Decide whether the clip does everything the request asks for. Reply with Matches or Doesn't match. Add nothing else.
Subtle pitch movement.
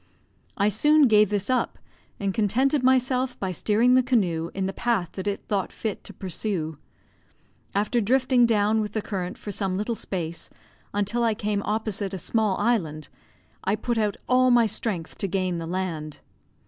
Doesn't match